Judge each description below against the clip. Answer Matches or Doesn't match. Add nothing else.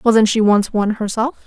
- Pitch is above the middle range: Matches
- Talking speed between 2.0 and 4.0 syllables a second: Doesn't match